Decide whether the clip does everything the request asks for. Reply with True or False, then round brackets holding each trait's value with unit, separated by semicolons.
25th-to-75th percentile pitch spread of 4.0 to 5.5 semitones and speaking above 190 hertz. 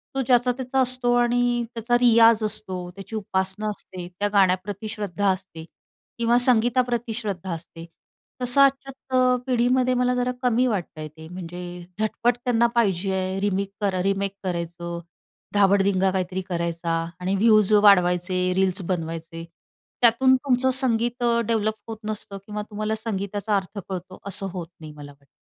True (4.6 semitones; 205 Hz)